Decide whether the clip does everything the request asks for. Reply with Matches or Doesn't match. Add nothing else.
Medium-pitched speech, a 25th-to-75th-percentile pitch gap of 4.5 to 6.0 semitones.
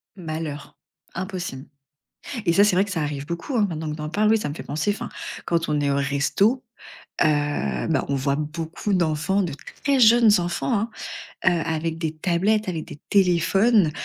Matches